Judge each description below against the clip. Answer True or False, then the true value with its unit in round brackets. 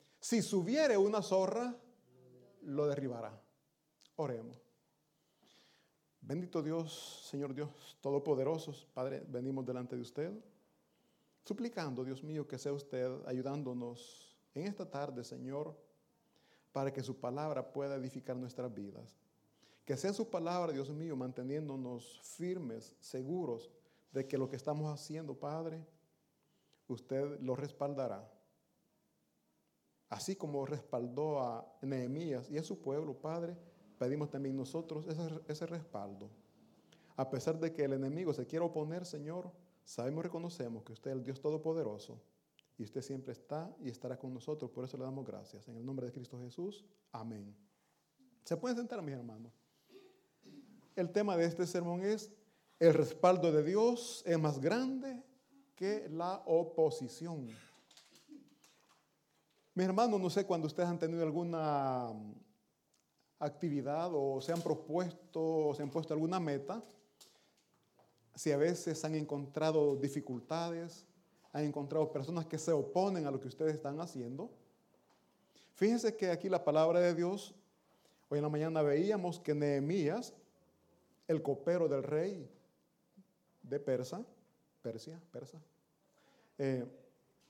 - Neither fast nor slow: True (130 wpm)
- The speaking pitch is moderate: True (155 Hz)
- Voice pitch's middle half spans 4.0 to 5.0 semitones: True (4.7 semitones)